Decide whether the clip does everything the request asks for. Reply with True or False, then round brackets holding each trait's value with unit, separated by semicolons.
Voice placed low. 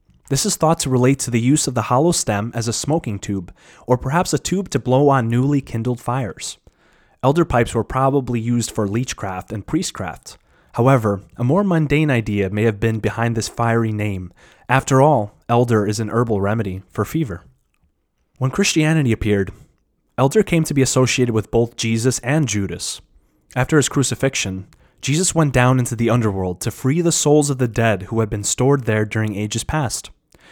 True (120 Hz)